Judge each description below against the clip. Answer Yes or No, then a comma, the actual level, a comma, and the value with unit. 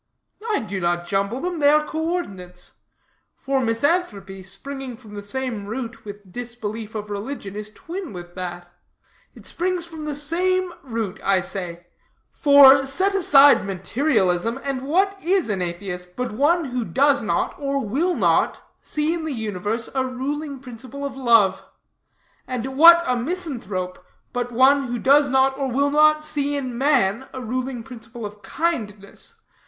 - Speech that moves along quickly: No, average, 155 wpm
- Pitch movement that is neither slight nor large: No, wide, 5.8 semitones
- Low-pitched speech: No, very high, 255 Hz